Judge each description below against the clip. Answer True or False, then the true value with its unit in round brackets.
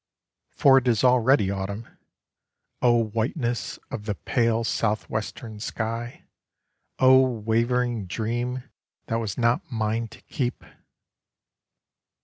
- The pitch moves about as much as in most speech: False (2.0 semitones)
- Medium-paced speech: False (105 wpm)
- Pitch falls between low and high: False (115 Hz)